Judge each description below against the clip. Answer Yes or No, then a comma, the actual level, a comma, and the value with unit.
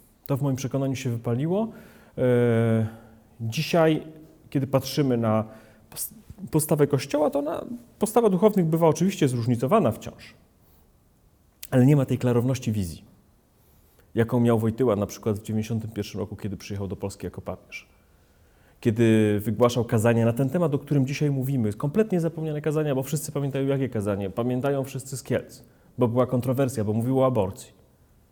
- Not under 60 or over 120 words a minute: No, average, 145 wpm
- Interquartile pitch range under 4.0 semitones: No, average, 4.9 semitones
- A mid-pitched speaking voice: No, low, 130 Hz